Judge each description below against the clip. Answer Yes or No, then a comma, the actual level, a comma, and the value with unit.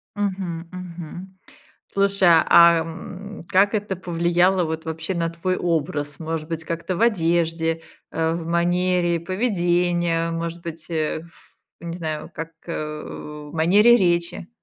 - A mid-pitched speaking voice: Yes, medium, 170 Hz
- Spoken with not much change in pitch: Yes, narrow, 1.9 semitones